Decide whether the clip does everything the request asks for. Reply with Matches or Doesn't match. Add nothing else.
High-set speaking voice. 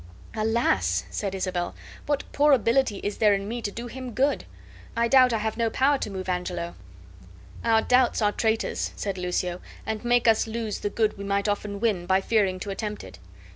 Matches